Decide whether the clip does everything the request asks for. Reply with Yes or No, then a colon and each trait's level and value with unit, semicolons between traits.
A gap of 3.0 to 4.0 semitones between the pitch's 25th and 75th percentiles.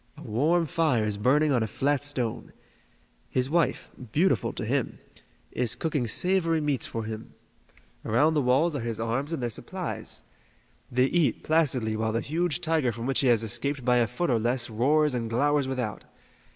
No: average, 4.6 semitones